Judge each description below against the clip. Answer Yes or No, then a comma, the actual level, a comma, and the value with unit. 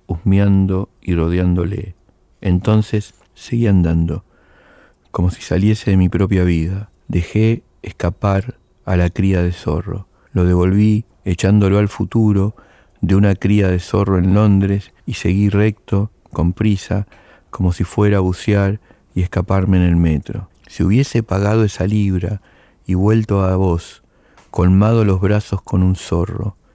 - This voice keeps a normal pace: Yes, average, 140 wpm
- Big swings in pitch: No, narrow, 2.4 semitones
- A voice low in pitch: Yes, very low, 95 Hz